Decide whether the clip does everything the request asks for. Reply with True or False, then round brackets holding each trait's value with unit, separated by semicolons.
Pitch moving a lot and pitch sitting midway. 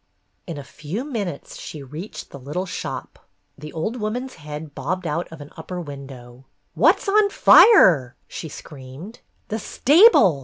True (7.0 semitones; 160 Hz)